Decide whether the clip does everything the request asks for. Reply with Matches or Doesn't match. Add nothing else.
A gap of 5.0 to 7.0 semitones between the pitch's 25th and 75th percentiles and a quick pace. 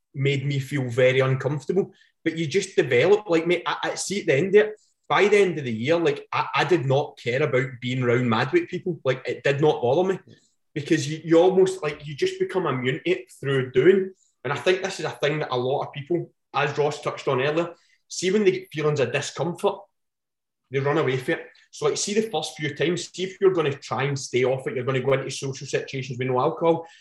Matches